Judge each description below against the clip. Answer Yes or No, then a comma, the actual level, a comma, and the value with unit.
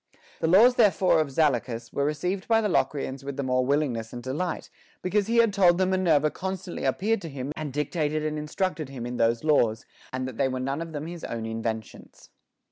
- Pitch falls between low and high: Yes, medium, 150 Hz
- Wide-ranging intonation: Yes, wide, 5.9 semitones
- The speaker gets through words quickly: Yes, fast, 210 wpm